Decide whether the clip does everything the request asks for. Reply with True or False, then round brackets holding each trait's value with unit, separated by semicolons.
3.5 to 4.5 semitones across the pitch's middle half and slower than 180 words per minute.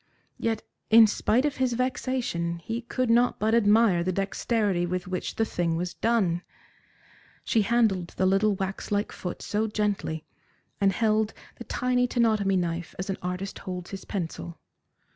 True (4.1 semitones; 160 wpm)